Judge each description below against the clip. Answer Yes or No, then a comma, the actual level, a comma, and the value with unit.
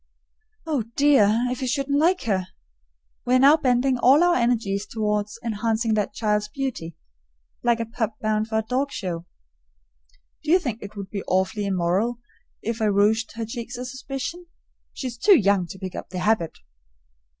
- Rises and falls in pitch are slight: No, average, 3.8 semitones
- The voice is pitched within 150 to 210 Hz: No, high, 225 Hz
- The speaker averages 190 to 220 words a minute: No, average, 175 wpm